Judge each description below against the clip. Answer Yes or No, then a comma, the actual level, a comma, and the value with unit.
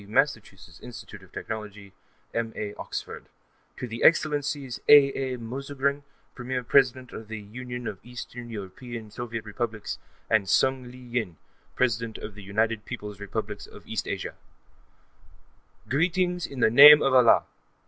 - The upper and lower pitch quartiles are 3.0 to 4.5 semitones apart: Yes, average, 3.7 semitones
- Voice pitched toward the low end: Yes, low, 120 Hz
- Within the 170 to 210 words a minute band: No, slow, 135 wpm